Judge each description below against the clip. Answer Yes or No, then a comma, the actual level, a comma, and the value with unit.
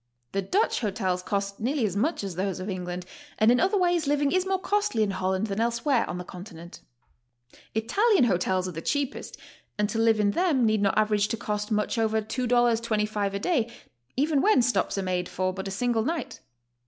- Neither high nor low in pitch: No, high, 220 Hz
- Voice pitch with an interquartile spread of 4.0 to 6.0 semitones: Yes, average, 4.8 semitones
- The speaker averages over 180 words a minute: Yes, average, 200 wpm